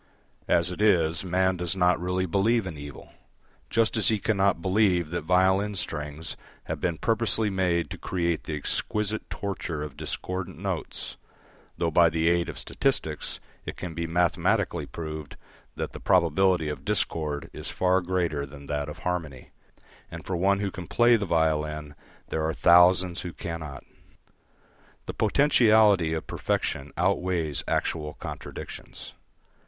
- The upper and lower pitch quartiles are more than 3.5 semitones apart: No, average, 3.1 semitones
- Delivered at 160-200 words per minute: No, average, 150 wpm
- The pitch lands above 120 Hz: No, very low, 85 Hz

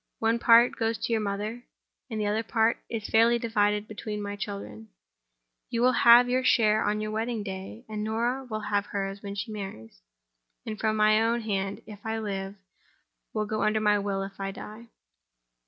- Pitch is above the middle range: Yes, high, 215 Hz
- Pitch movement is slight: Yes, narrow, 2.0 semitones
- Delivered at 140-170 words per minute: No, average, 180 wpm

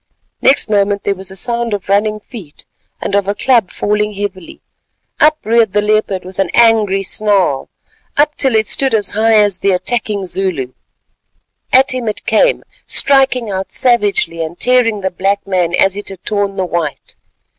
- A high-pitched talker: Yes, high, 205 Hz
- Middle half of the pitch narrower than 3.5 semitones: Yes, average, 3.0 semitones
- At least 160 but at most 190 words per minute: Yes, average, 175 wpm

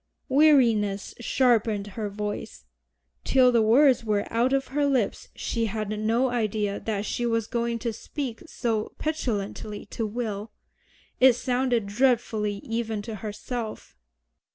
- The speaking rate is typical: No, slow, 130 wpm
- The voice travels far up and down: No, average, 2.9 semitones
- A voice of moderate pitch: No, high, 225 Hz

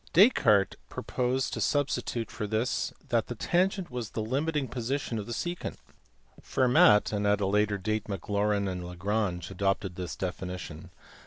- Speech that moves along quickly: No, average, 150 wpm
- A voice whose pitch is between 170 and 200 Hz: No, low, 105 Hz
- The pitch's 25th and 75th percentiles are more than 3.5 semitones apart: Yes, average, 4.5 semitones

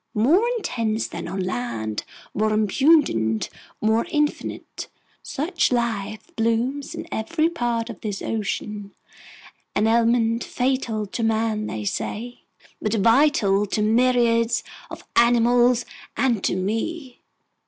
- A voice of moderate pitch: No, high, 230 Hz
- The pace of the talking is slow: Yes, slow, 110 wpm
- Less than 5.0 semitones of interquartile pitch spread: Yes, narrow, 2.6 semitones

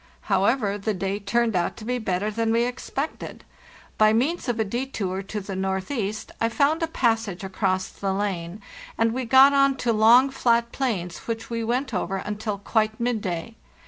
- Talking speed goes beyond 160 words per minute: Yes, average, 175 wpm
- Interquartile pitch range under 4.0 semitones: Yes, average, 3.6 semitones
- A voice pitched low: No, high, 220 Hz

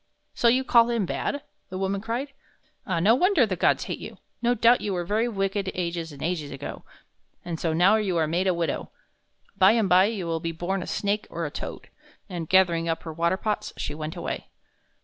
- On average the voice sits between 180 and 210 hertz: Yes, medium, 185 Hz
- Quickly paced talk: Yes, fast, 215 wpm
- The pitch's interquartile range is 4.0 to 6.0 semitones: Yes, average, 4.3 semitones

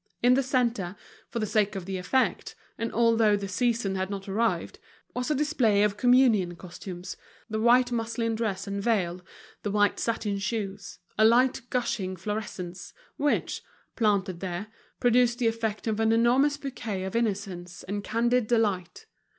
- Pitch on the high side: Yes, high, 220 Hz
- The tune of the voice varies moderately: Yes, average, 3.5 semitones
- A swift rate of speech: No, average, 160 wpm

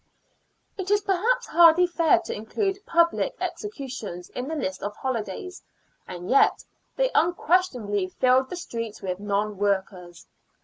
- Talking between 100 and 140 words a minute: Yes, slow, 135 wpm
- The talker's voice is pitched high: Yes, very high, 260 Hz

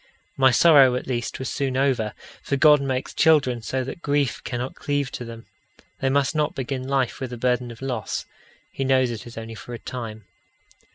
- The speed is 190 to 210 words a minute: Yes, average, 195 wpm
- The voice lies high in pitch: No, low, 130 Hz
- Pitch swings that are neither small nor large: No, narrow, 2.3 semitones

